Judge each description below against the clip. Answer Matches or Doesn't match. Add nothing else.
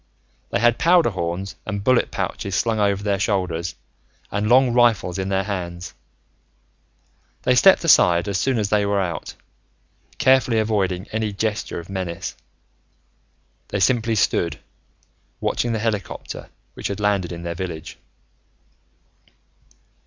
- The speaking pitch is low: Matches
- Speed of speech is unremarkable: Doesn't match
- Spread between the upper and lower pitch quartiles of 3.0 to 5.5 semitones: Matches